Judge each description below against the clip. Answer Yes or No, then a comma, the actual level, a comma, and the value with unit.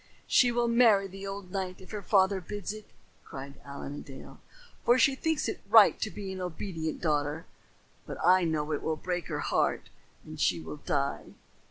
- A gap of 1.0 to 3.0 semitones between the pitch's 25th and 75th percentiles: No, average, 4.8 semitones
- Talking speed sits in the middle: Yes, average, 190 wpm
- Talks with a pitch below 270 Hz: Yes, medium, 185 Hz